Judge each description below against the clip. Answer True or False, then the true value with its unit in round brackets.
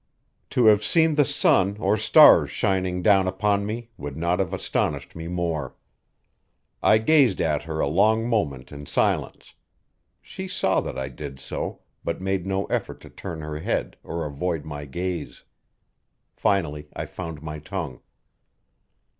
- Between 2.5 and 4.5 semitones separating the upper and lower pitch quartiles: False (4.9 semitones)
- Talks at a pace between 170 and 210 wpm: False (155 wpm)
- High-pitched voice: False (90 Hz)